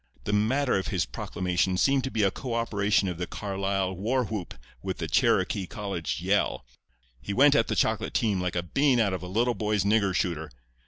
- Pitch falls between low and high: No, low, 100 Hz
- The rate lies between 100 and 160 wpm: No, fast, 205 wpm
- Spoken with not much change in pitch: No, average, 3.7 semitones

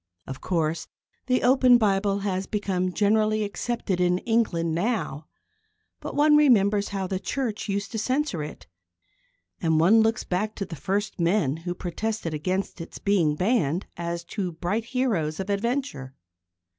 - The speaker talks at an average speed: Yes, average, 150 wpm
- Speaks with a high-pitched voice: Yes, high, 195 Hz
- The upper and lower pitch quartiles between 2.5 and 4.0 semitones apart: No, average, 4.5 semitones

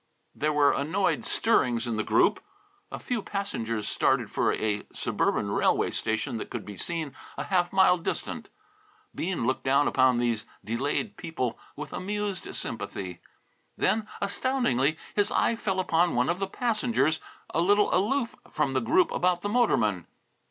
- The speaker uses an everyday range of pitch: No, wide, 8.5 semitones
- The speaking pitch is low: No, medium, 170 Hz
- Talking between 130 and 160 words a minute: Yes, average, 155 wpm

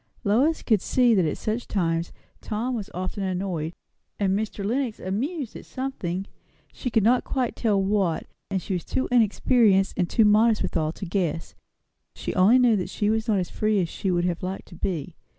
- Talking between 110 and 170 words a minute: No, average, 195 wpm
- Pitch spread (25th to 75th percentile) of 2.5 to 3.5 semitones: No, average, 3.9 semitones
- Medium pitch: No, high, 200 Hz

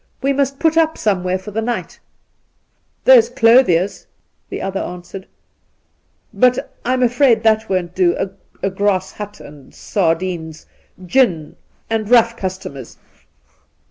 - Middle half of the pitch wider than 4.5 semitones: Yes, average, 5.1 semitones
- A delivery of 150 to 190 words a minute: No, average, 140 wpm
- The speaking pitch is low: No, high, 205 Hz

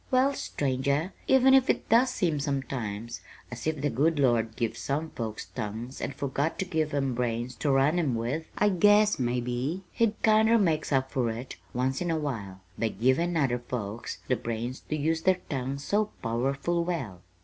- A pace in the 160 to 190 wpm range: Yes, average, 180 wpm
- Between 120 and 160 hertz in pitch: Yes, medium, 140 Hz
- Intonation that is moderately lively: No, wide, 5.7 semitones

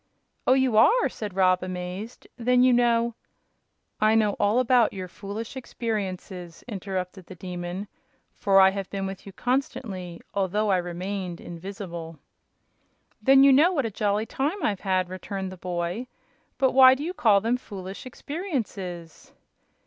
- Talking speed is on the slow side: No, average, 155 wpm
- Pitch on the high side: Yes, high, 200 Hz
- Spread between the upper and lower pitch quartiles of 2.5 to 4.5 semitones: No, average, 4.9 semitones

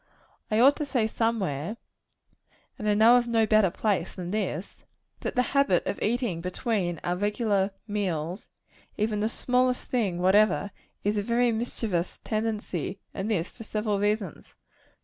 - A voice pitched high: Yes, high, 210 Hz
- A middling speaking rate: Yes, average, 150 wpm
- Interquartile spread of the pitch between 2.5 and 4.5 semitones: Yes, average, 3.3 semitones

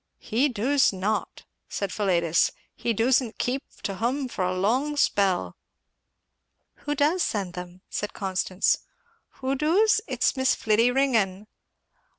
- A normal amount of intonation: No, wide, 5.9 semitones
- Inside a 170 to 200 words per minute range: No, slow, 135 wpm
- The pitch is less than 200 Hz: No, high, 225 Hz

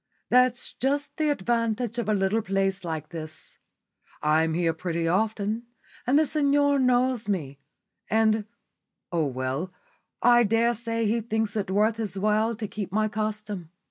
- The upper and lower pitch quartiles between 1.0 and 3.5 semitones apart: No, average, 4.0 semitones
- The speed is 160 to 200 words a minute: No, average, 145 wpm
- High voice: Yes, high, 215 Hz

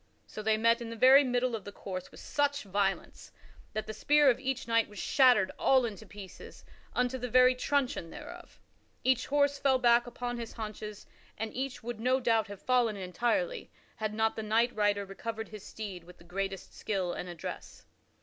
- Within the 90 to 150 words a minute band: No, average, 190 wpm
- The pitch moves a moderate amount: Yes, average, 3.6 semitones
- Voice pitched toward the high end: Yes, high, 230 Hz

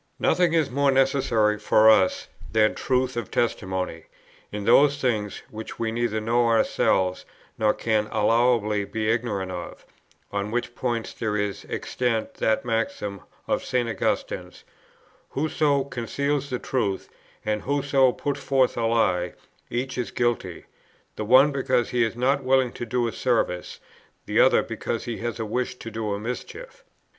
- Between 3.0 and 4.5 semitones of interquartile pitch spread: Yes, average, 3.3 semitones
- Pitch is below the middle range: Yes, low, 115 Hz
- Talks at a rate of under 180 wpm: Yes, average, 155 wpm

